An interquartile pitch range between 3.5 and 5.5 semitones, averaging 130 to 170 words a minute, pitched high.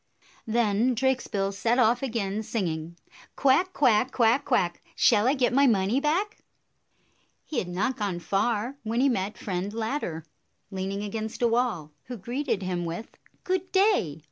Yes: average, 5.0 semitones; average, 155 wpm; high, 225 Hz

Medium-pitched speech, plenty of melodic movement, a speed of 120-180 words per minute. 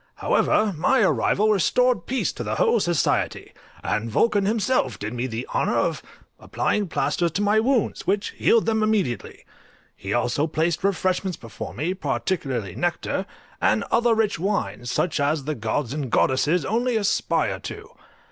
Yes: medium, 180 Hz; wide, 8.5 semitones; average, 155 wpm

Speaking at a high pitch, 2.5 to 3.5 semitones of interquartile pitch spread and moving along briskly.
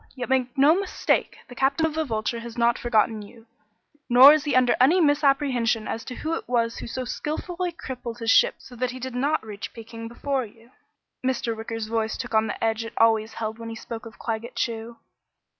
Yes: high, 240 Hz; average, 2.9 semitones; fast, 210 wpm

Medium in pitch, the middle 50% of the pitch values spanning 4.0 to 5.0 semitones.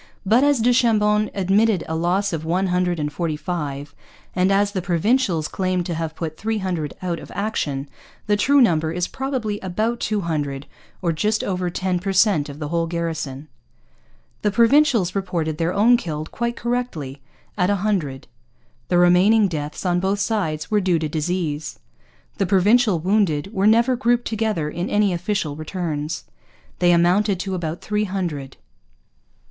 Yes: medium, 180 Hz; average, 4.6 semitones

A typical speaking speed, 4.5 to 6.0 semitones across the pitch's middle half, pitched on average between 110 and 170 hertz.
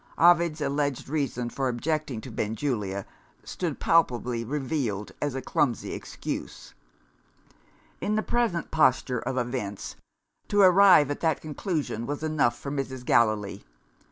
No: slow, 130 wpm; average, 4.8 semitones; low, 135 Hz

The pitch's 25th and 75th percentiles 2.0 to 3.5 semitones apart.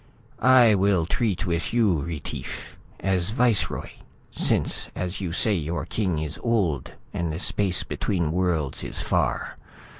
No: average, 4.1 semitones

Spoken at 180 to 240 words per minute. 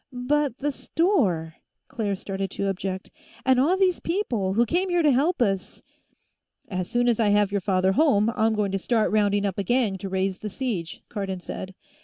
Yes: average, 200 wpm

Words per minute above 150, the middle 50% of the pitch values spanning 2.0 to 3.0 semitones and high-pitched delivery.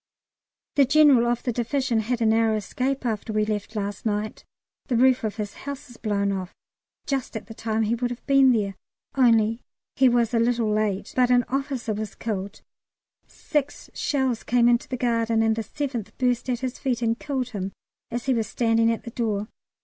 Yes: average, 195 wpm; narrow, 2.6 semitones; high, 235 Hz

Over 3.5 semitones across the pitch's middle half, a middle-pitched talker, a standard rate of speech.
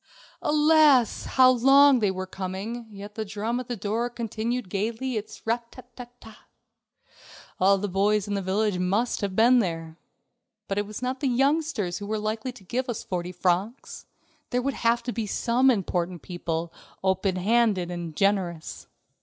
No: average, 4.3 semitones; high, 215 Hz; average, 175 wpm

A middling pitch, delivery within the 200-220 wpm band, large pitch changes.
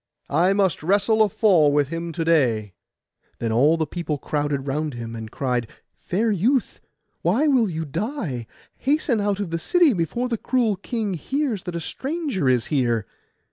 No: medium, 170 Hz; average, 175 wpm; wide, 7.5 semitones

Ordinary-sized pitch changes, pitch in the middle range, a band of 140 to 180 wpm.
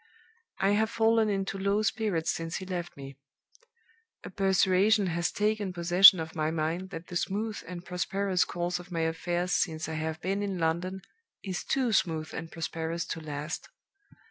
Yes: average, 3.1 semitones; medium, 180 Hz; average, 170 wpm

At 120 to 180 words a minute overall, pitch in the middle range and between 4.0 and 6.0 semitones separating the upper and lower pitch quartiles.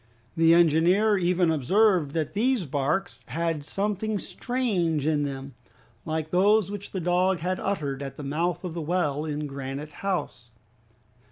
Yes: average, 150 wpm; medium, 170 Hz; average, 4.5 semitones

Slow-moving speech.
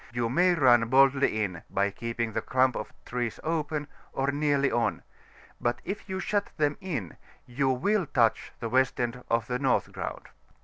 No: average, 175 wpm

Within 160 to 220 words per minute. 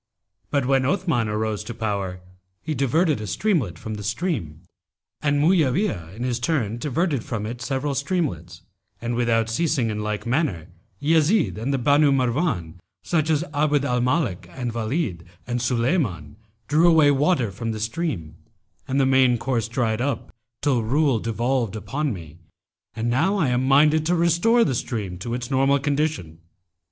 Yes: average, 165 wpm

